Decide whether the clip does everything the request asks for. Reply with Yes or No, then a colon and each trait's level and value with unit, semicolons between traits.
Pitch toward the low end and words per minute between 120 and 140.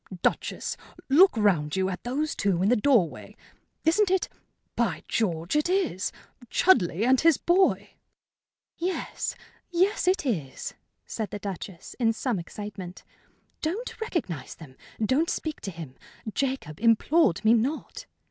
No: high, 230 Hz; slow, 135 wpm